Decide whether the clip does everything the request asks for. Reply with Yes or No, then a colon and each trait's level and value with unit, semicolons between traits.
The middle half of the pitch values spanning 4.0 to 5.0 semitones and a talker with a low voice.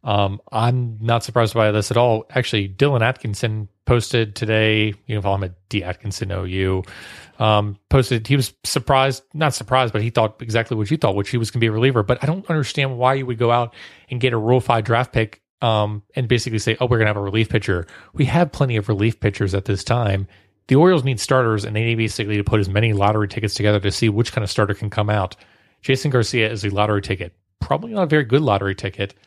No: average, 3.4 semitones; low, 110 Hz